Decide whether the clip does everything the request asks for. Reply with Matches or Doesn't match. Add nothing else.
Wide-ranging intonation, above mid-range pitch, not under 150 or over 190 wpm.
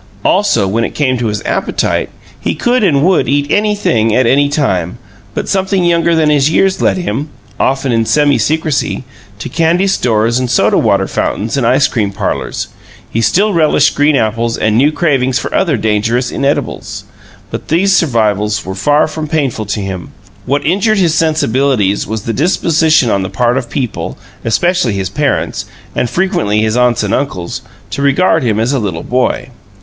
Doesn't match